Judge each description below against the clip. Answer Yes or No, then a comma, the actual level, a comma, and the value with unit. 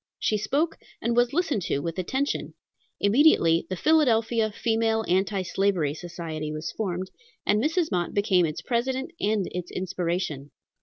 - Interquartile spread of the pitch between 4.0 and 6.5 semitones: Yes, average, 5.3 semitones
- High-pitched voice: Yes, high, 200 Hz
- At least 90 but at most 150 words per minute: Yes, average, 145 wpm